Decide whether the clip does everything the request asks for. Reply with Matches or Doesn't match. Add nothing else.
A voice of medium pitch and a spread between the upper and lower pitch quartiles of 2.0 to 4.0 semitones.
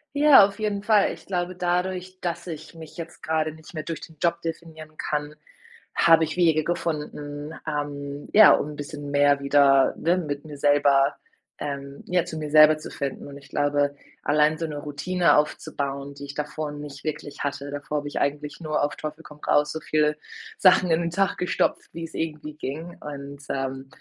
Matches